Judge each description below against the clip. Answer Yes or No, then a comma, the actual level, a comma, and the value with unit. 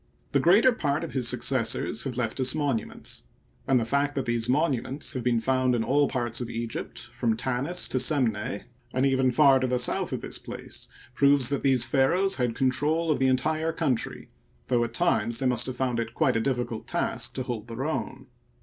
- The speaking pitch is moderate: No, low, 130 Hz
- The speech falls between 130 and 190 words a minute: No, fast, 205 wpm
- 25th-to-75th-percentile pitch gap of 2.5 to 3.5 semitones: Yes, average, 2.9 semitones